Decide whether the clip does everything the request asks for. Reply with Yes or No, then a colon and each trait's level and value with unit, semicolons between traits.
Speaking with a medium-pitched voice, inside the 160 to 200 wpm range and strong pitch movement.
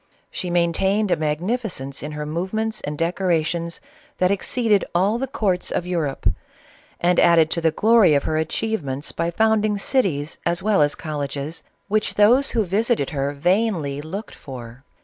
Yes: medium, 175 Hz; average, 170 wpm; wide, 5.8 semitones